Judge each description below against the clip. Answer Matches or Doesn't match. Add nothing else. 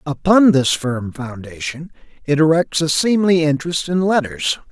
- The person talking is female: Doesn't match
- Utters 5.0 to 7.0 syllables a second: Doesn't match